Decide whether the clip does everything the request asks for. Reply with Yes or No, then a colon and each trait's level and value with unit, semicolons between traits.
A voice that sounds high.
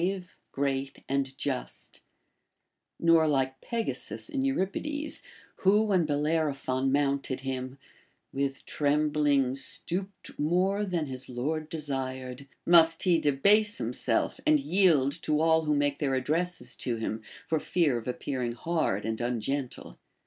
No: medium, 145 Hz